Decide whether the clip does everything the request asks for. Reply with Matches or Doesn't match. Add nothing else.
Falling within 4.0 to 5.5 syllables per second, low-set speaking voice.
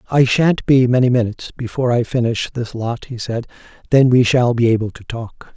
Matches